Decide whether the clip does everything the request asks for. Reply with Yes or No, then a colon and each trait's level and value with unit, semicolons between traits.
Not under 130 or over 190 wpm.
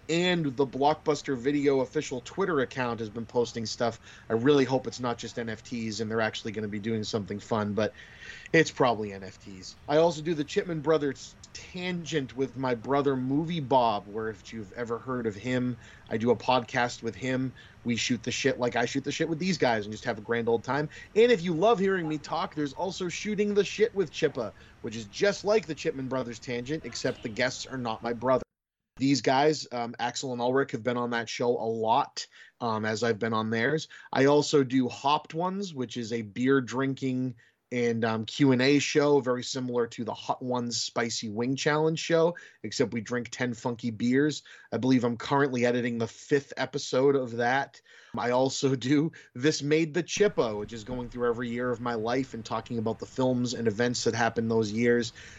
No: fast, 205 wpm